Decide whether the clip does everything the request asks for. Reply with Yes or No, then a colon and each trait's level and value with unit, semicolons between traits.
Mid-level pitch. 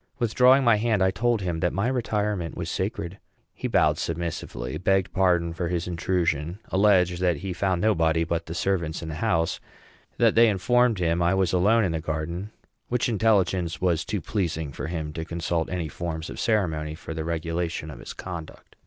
No: very low, 90 Hz